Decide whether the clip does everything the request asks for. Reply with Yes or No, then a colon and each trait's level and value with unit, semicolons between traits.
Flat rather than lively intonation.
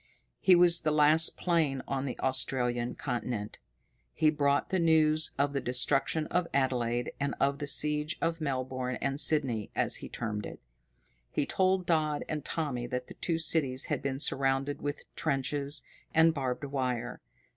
No: average, 3.3 semitones